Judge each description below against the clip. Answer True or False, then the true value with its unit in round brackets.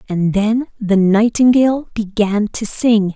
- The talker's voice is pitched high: True (215 Hz)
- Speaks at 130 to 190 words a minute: True (135 wpm)